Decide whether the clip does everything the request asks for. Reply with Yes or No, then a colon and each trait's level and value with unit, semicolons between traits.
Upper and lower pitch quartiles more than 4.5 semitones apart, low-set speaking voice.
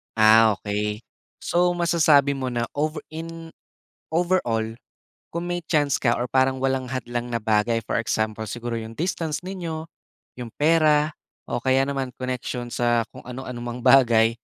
Yes: average, 4.9 semitones; low, 130 Hz